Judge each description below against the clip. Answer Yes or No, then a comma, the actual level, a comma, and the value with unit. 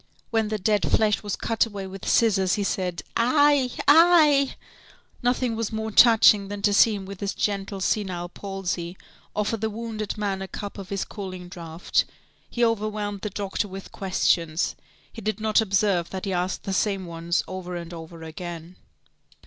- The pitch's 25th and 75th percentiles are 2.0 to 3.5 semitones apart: Yes, average, 3.0 semitones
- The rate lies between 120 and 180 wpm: Yes, average, 175 wpm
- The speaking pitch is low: No, high, 200 Hz